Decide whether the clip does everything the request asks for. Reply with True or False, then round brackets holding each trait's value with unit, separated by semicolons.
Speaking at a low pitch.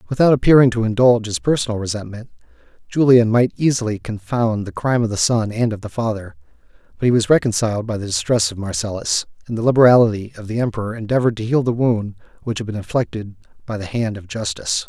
True (110 Hz)